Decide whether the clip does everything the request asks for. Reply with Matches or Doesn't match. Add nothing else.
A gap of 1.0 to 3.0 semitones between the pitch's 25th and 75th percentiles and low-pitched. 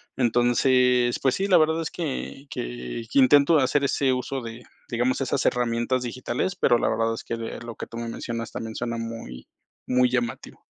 Matches